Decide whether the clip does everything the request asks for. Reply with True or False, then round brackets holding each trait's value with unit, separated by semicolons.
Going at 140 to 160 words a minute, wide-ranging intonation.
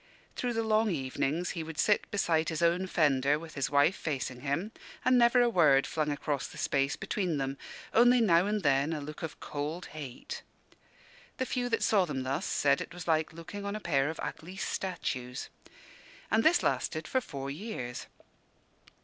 False (185 wpm; 6.1 semitones)